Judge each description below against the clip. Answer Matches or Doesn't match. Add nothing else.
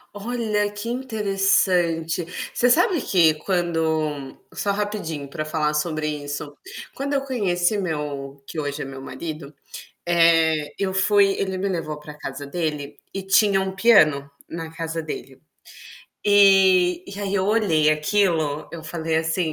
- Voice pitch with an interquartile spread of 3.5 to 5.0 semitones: Matches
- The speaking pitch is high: Doesn't match